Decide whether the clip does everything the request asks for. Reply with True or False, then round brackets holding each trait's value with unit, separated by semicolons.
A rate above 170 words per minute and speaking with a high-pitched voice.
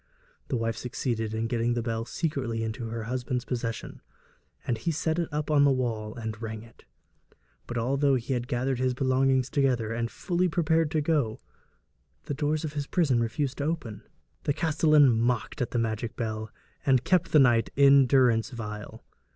False (185 wpm; 125 Hz)